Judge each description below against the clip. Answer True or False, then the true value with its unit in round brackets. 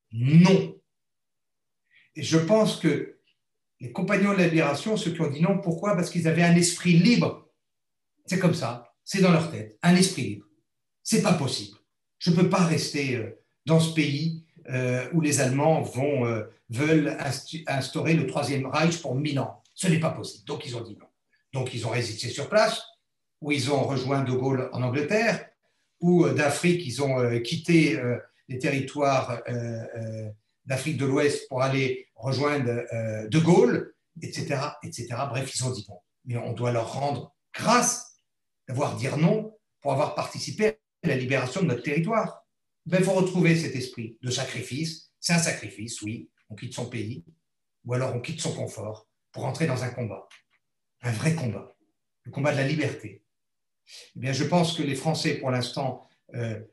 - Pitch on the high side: False (140 Hz)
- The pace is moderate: True (170 wpm)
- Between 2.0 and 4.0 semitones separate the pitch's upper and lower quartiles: False (5.1 semitones)